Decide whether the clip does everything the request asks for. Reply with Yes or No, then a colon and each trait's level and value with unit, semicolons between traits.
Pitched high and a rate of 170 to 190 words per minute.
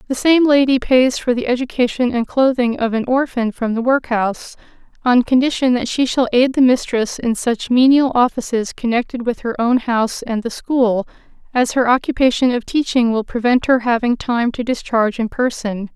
Yes: high, 245 Hz; average, 185 wpm